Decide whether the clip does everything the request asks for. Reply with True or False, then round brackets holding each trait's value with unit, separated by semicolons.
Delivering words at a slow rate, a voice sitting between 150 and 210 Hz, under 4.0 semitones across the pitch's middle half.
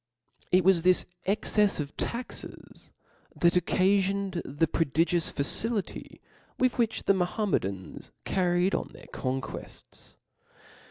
True (120 wpm; 185 Hz; 3.4 semitones)